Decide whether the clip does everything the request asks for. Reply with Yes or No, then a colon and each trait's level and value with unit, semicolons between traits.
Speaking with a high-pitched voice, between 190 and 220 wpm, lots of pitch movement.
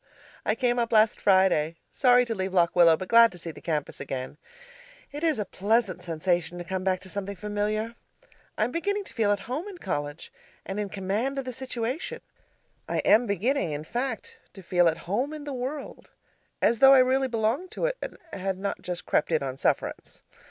Yes: high, 210 Hz; fast, 205 wpm; wide, 6.0 semitones